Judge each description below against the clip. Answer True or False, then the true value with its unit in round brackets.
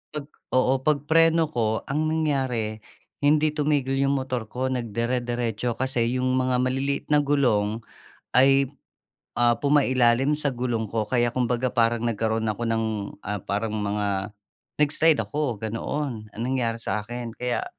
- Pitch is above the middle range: False (125 Hz)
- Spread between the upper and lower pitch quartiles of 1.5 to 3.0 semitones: False (3.4 semitones)